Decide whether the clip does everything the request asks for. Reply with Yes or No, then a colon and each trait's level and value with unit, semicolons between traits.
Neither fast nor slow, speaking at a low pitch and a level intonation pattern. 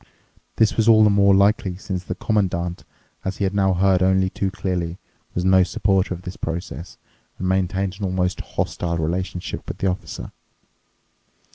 Yes: average, 165 wpm; very low, 95 Hz; narrow, 1.5 semitones